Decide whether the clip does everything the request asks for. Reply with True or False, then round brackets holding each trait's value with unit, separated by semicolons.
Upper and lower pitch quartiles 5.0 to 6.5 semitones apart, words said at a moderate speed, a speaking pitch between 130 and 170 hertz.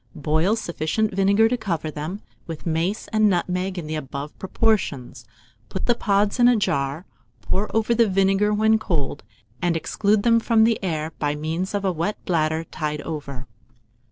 False (5.4 semitones; 170 wpm; 185 Hz)